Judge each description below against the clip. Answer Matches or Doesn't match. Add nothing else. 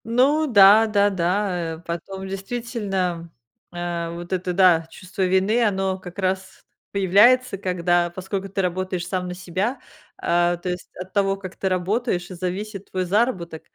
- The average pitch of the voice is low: Doesn't match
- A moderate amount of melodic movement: Doesn't match